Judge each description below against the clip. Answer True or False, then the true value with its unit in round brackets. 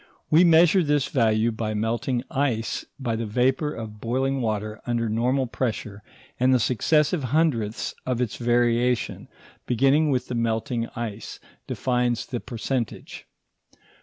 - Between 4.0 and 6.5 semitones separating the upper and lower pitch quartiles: False (2.9 semitones)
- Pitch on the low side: True (120 Hz)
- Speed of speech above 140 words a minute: False (135 wpm)